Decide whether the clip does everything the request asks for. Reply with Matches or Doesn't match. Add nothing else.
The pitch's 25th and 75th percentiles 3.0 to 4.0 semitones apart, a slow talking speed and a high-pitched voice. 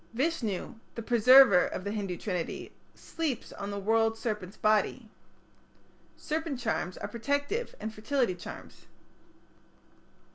Doesn't match